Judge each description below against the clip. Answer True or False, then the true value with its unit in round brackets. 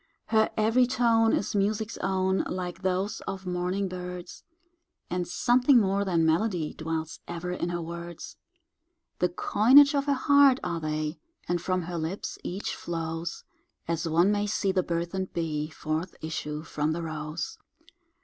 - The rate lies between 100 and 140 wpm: False (150 wpm)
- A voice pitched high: False (180 Hz)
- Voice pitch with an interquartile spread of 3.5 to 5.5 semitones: True (3.8 semitones)